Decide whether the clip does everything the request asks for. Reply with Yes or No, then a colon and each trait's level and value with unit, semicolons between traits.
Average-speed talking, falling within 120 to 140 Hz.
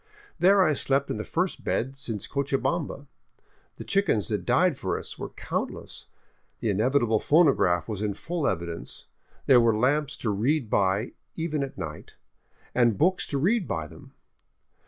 Yes: average, 155 wpm; low, 135 Hz